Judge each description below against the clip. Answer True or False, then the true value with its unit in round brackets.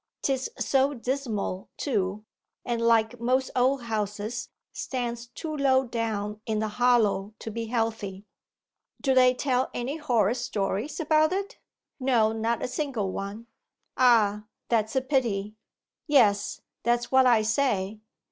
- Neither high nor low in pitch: False (235 Hz)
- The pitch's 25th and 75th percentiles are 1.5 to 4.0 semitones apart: True (3.6 semitones)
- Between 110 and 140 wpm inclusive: True (135 wpm)